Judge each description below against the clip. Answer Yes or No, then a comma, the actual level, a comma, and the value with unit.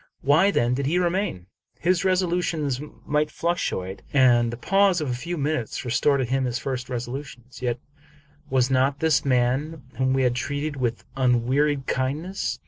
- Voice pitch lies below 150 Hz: Yes, low, 135 Hz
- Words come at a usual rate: Yes, average, 170 wpm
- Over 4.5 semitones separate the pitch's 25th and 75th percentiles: No, average, 4.0 semitones